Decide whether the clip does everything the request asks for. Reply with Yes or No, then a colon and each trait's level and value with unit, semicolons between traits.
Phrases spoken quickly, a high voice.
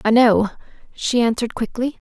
No: average, 140 wpm; high, 235 Hz